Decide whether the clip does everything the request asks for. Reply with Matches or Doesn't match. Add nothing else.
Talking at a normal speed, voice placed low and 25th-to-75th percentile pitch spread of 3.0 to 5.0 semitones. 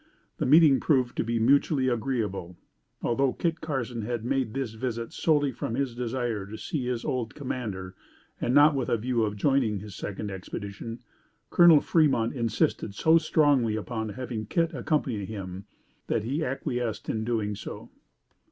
Matches